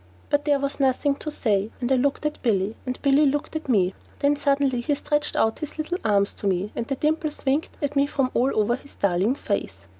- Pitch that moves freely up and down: No, average, 4.8 semitones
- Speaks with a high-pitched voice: Yes, very high, 270 Hz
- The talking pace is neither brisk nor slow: No, fast, 230 wpm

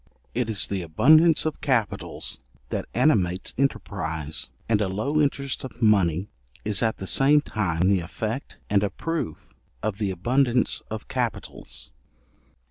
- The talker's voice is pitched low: Yes, low, 105 Hz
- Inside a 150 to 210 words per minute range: No, average, 140 wpm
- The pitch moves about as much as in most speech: No, wide, 6.3 semitones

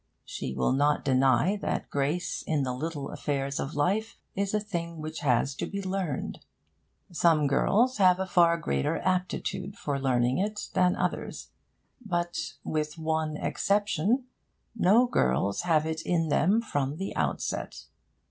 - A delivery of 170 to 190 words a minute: No, average, 150 wpm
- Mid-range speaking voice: Yes, medium, 165 Hz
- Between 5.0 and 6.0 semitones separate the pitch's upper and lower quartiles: Yes, average, 5.3 semitones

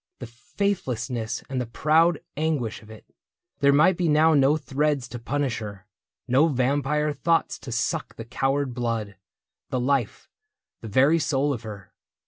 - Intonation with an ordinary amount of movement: Yes, average, 4.3 semitones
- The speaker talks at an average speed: Yes, average, 155 wpm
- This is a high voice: No, low, 135 Hz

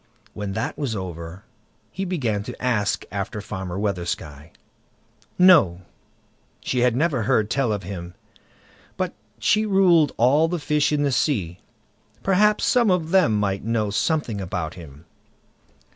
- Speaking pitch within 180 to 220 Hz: No, low, 110 Hz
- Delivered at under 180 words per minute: Yes, average, 140 wpm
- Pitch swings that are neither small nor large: No, wide, 8.5 semitones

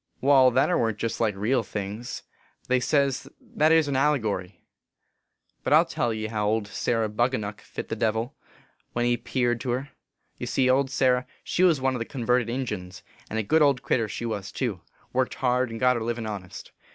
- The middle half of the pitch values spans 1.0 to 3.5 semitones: Yes, average, 3.2 semitones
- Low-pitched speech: Yes, low, 120 Hz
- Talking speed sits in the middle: No, fast, 215 wpm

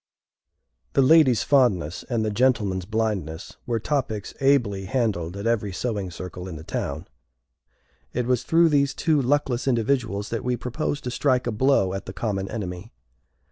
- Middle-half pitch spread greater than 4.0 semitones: Yes, average, 5.1 semitones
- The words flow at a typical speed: Yes, average, 160 wpm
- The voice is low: Yes, low, 115 Hz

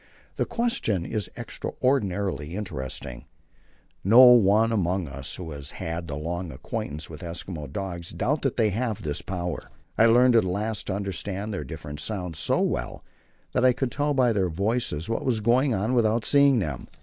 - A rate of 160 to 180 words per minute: Yes, average, 170 wpm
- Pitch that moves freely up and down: Yes, wide, 5.9 semitones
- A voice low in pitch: Yes, low, 100 Hz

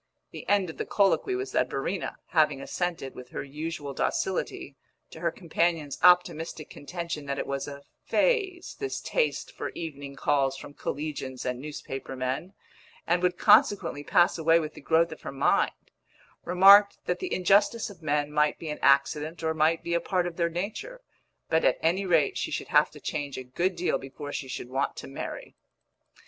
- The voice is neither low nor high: Yes, medium, 160 Hz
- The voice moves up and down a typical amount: Yes, average, 4.0 semitones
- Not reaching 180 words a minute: No, average, 185 wpm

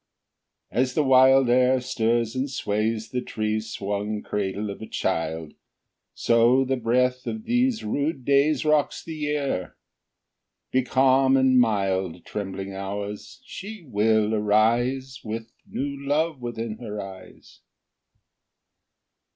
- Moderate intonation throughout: Yes, average, 4.1 semitones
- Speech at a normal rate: No, slow, 125 wpm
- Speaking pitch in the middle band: No, low, 120 Hz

